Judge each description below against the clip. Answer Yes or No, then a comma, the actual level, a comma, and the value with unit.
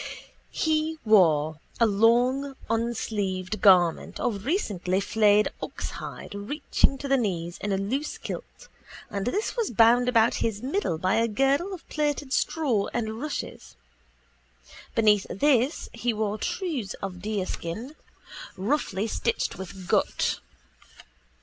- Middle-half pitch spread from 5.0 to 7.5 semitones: Yes, wide, 5.5 semitones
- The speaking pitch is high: Yes, high, 225 Hz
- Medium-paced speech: No, slow, 125 wpm